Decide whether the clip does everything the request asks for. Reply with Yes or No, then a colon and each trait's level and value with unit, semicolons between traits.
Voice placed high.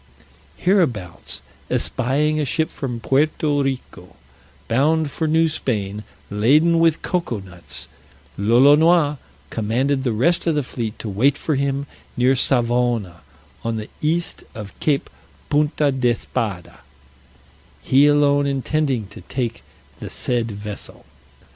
No: low, 135 Hz